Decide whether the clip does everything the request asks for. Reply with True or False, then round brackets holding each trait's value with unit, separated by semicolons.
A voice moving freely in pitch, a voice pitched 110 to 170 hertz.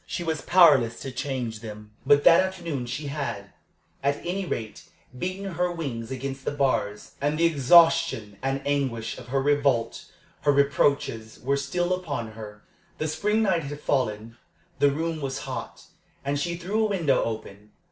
True (5.8 semitones; 140 Hz)